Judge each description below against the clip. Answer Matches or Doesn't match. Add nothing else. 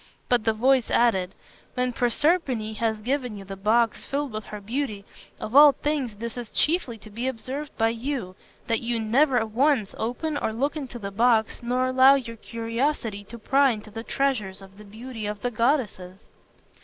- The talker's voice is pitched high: Matches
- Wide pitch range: Doesn't match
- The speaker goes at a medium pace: Matches